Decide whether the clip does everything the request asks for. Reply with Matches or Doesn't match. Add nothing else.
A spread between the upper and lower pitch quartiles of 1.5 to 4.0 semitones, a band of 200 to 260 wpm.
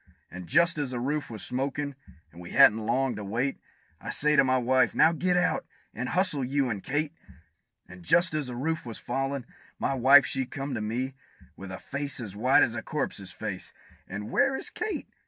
Doesn't match